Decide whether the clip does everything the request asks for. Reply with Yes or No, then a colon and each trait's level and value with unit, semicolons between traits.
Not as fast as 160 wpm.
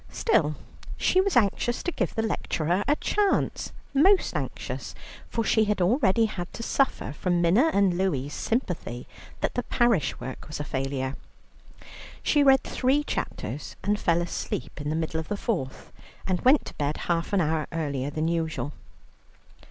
No: average, 165 wpm